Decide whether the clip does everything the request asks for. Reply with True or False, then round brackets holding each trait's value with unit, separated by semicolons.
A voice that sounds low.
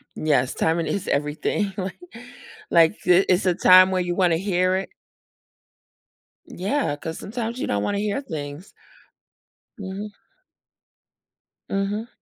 False (185 Hz)